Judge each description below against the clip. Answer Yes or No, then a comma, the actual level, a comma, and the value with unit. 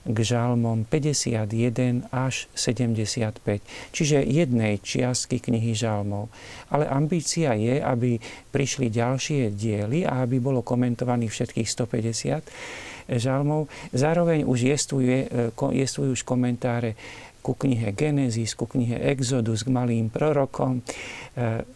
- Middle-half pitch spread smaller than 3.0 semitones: Yes, narrow, 2.6 semitones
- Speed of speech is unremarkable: No, slow, 100 wpm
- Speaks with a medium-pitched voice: No, low, 125 Hz